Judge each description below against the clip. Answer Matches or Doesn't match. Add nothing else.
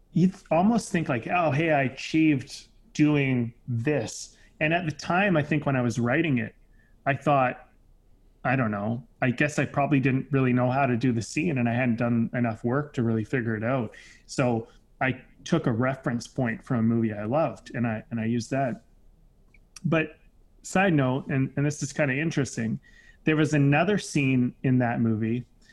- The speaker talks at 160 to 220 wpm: Matches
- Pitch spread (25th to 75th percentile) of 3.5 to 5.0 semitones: Matches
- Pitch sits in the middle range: Doesn't match